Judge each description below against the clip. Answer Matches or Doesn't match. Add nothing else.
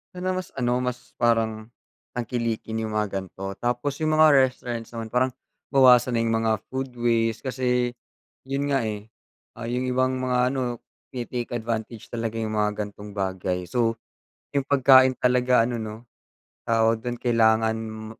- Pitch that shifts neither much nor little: Doesn't match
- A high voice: Doesn't match